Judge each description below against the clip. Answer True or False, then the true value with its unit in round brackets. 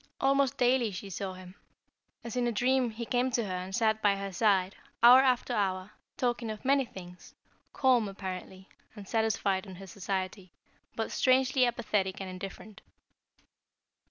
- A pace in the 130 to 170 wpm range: True (155 wpm)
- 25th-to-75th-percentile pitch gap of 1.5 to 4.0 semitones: False (4.4 semitones)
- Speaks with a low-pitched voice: False (210 Hz)